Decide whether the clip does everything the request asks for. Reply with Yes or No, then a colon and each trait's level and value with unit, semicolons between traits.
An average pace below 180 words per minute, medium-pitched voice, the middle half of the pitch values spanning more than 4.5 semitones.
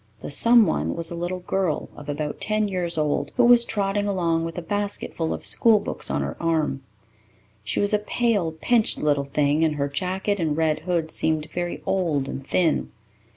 No: average, 190 wpm; medium, 170 Hz; average, 4.9 semitones